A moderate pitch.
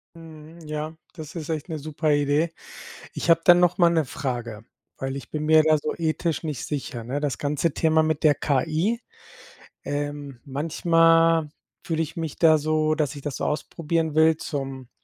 Yes: medium, 155 Hz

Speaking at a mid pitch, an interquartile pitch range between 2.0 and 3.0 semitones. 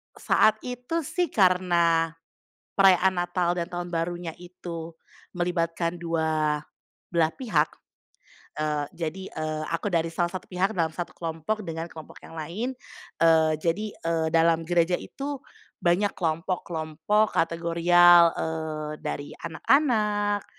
Yes: medium, 170 Hz; narrow, 2.4 semitones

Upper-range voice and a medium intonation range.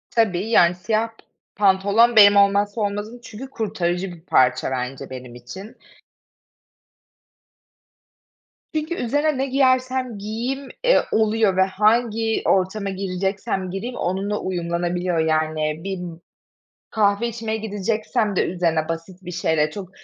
Yes: high, 200 Hz; average, 4.0 semitones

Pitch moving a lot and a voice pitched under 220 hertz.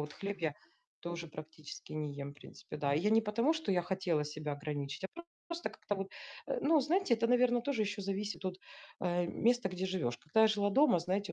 Yes: wide, 6.5 semitones; high, 190 Hz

